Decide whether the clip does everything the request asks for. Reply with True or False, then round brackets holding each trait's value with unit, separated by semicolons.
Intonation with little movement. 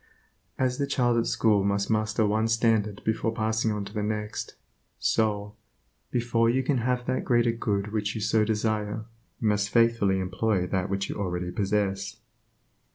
True (2.2 semitones)